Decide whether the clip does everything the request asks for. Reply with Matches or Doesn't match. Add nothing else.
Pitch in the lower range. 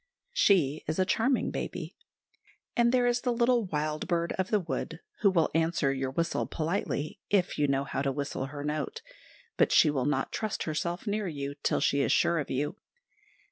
Doesn't match